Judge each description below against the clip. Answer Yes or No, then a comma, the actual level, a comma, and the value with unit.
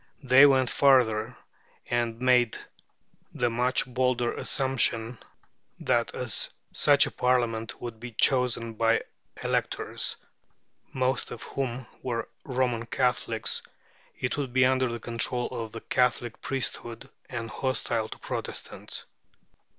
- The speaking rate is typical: No, slow, 120 wpm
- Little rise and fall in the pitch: Yes, narrow, 1.8 semitones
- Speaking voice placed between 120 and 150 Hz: Yes, low, 125 Hz